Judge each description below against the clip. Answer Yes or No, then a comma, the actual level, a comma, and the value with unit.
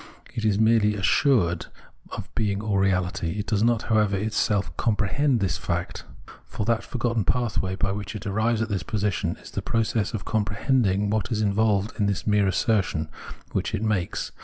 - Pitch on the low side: Yes, low, 105 Hz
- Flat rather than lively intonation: Yes, narrow, 2.3 semitones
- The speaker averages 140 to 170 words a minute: No, average, 185 wpm